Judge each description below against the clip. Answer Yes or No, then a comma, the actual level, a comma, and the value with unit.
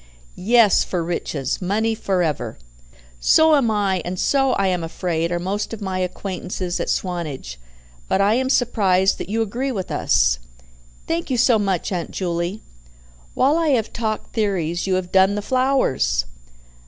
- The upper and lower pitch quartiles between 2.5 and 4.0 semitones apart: No, average, 4.4 semitones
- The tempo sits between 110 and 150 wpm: No, average, 165 wpm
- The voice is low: No, high, 195 Hz